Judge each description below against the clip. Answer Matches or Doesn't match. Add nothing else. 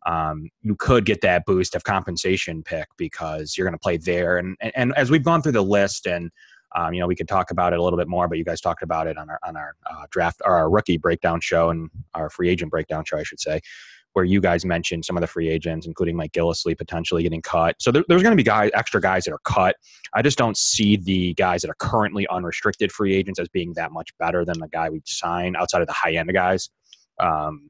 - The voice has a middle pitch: Doesn't match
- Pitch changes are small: Doesn't match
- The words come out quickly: Matches